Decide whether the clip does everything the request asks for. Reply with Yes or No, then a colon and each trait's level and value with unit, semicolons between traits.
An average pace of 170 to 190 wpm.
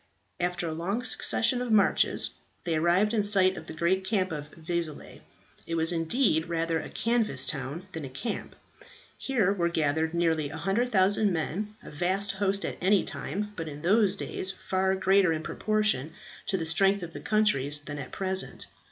Yes: average, 175 wpm